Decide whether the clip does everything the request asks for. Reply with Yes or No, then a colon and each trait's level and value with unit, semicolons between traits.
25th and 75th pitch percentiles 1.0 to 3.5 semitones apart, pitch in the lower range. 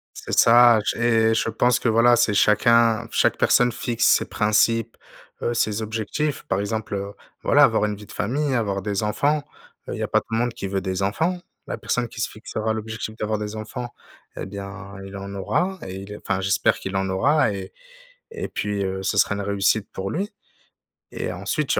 Yes: average, 2.9 semitones; low, 110 Hz